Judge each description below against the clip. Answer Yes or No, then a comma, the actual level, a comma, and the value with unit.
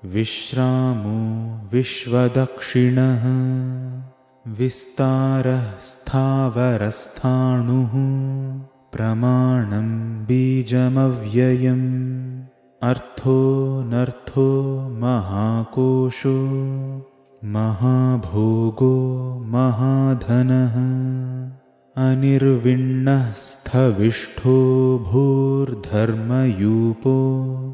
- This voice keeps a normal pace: No, slow, 30 wpm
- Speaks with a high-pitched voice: No, low, 130 Hz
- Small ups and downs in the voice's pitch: Yes, narrow, 1.3 semitones